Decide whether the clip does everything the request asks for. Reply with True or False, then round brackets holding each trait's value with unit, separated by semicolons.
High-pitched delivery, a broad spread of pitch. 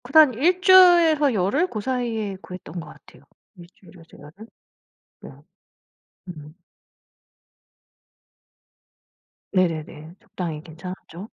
True (195 Hz; 8.6 semitones)